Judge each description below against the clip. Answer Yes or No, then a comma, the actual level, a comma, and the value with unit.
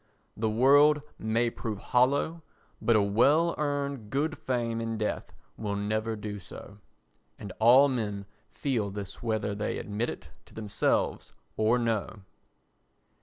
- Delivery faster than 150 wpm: No, slow, 135 wpm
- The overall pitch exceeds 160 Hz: No, low, 115 Hz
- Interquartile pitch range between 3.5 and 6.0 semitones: Yes, average, 4.0 semitones